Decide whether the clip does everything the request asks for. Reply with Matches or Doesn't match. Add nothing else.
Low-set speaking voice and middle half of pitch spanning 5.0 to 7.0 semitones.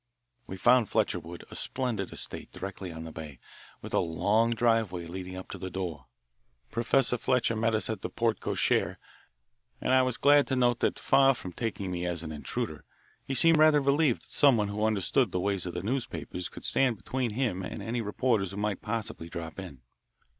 Matches